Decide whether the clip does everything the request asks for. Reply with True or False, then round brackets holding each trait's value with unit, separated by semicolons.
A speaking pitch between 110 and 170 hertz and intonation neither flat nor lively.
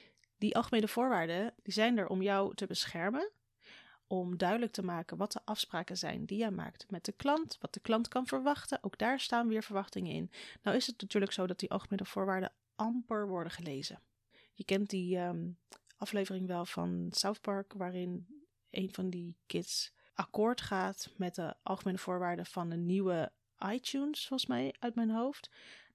False (195 Hz; 3.9 semitones)